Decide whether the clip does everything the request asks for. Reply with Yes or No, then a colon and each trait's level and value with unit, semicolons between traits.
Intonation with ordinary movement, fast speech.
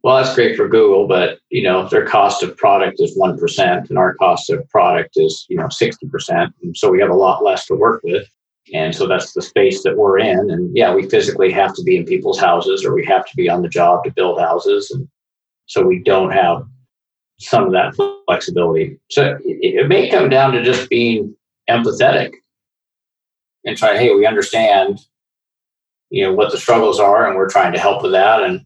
Yes: average, 3.3 semitones; fast, 210 wpm